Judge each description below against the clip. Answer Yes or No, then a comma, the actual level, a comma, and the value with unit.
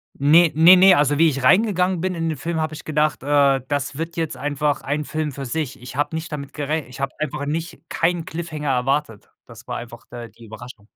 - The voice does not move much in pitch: No, average, 3.2 semitones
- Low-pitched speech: No, medium, 150 Hz